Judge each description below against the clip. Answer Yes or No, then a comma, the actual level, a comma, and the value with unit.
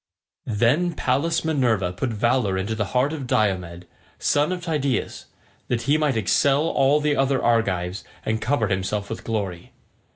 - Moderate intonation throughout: No, wide, 5.9 semitones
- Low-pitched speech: Yes, low, 120 Hz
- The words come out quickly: No, average, 155 wpm